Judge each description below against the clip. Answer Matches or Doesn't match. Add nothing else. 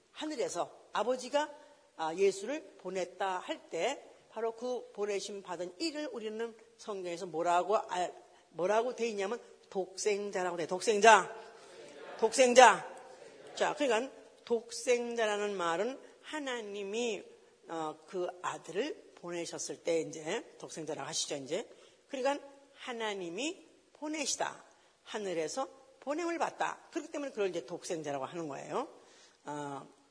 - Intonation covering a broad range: Matches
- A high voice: Matches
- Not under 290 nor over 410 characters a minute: Doesn't match